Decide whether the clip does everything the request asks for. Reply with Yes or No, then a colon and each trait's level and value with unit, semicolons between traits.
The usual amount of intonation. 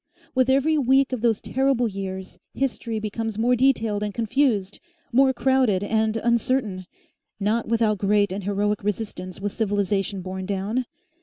Yes: average, 3.6 semitones